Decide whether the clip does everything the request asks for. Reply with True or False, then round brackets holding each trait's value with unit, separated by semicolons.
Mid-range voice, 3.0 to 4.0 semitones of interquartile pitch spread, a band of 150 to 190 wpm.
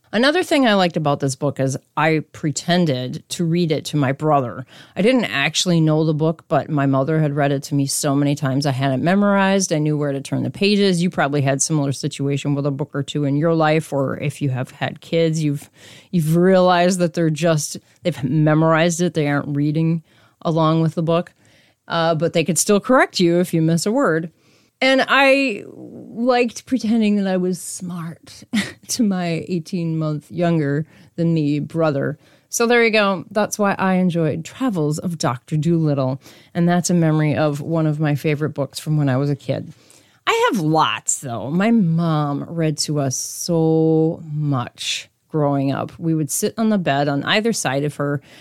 False (160 Hz; 3.6 semitones; 200 wpm)